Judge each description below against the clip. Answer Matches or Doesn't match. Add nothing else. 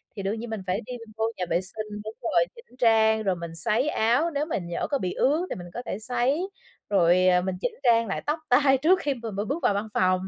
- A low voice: Doesn't match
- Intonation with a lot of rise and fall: Matches